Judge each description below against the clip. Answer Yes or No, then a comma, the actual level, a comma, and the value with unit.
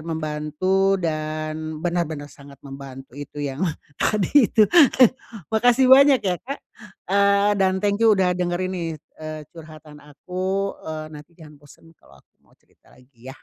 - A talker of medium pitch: Yes, medium, 165 Hz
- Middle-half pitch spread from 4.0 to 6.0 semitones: Yes, average, 4.4 semitones